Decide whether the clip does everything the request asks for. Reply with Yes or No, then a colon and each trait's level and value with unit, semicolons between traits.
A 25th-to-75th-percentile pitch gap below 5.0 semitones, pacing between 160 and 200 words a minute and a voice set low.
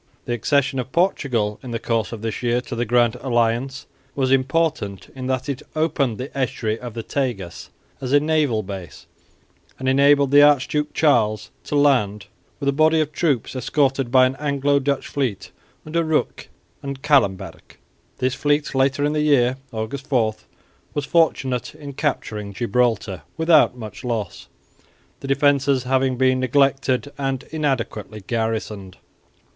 No: average, 3.6 semitones; average, 150 wpm; low, 130 Hz